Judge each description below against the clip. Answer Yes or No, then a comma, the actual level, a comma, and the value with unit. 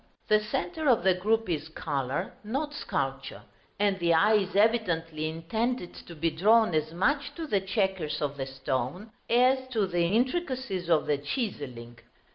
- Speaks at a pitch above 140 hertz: Yes, high, 190 Hz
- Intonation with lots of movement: Yes, wide, 6.1 semitones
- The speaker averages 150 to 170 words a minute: Yes, average, 160 wpm